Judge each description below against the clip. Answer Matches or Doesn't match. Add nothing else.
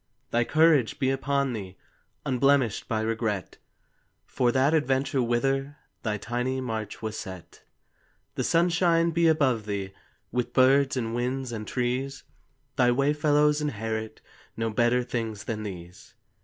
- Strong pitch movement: Doesn't match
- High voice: Doesn't match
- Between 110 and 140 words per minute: Matches